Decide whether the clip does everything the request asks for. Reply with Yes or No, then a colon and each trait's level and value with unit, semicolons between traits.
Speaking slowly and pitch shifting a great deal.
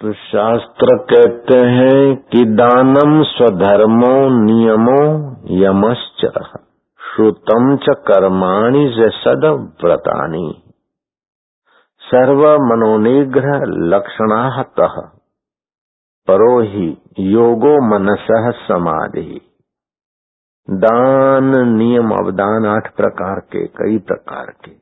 No: slow, 70 wpm; average, 4.0 semitones